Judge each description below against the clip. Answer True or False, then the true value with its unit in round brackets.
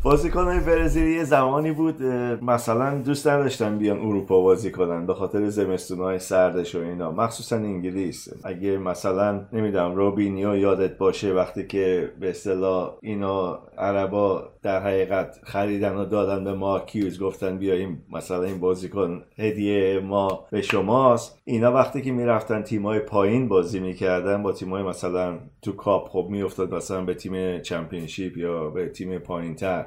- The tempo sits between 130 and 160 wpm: True (150 wpm)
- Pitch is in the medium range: False (100 Hz)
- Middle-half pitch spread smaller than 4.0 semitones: True (2.9 semitones)